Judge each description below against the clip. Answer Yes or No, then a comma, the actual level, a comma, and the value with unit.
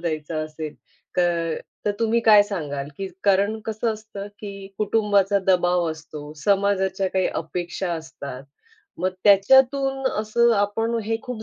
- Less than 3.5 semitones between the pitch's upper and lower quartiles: No, average, 4.0 semitones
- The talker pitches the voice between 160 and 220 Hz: Yes, high, 200 Hz